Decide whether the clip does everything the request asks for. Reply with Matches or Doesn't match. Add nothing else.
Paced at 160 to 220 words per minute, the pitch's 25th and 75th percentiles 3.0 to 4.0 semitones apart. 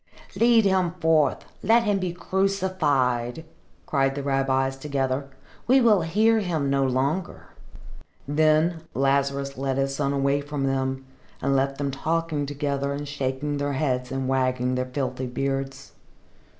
Doesn't match